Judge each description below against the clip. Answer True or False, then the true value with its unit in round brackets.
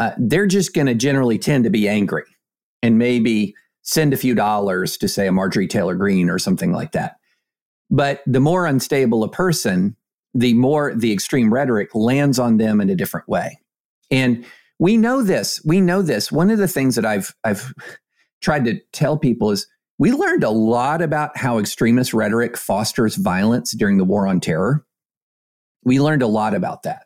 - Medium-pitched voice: False (120 Hz)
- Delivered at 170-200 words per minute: True (185 wpm)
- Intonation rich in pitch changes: True (5.8 semitones)